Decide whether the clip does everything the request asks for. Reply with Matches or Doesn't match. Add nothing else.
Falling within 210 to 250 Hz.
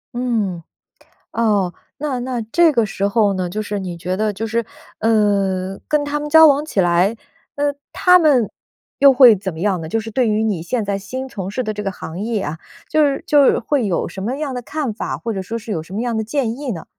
Matches